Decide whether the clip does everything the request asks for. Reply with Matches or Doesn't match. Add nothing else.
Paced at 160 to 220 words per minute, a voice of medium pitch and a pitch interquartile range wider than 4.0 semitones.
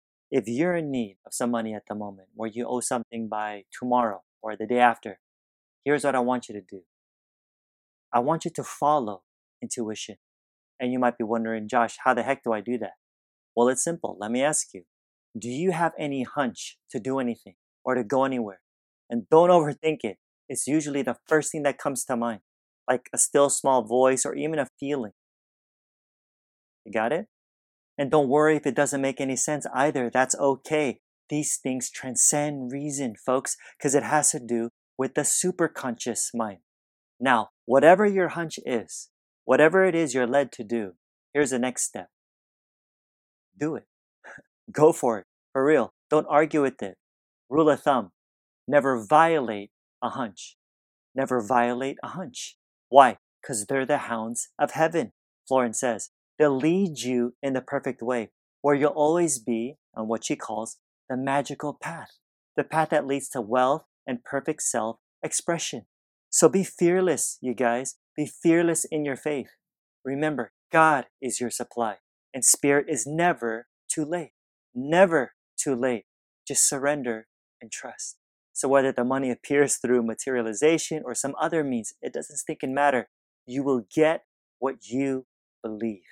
Doesn't match